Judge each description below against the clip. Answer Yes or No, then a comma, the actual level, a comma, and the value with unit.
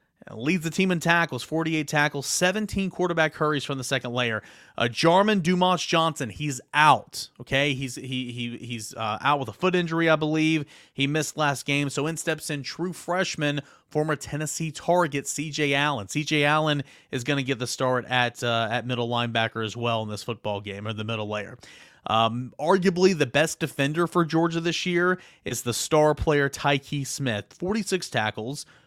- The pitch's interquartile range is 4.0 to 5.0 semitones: Yes, average, 4.7 semitones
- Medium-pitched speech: Yes, medium, 145 Hz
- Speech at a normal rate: Yes, average, 185 wpm